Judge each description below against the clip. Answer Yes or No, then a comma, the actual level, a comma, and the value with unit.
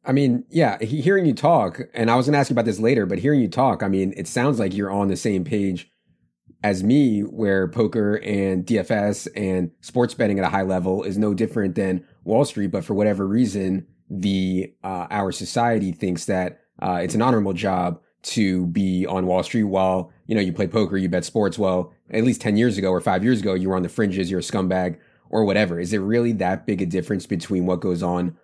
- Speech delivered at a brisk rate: Yes, fast, 230 wpm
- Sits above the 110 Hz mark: No, very low, 95 Hz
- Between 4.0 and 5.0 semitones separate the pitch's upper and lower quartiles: No, average, 2.9 semitones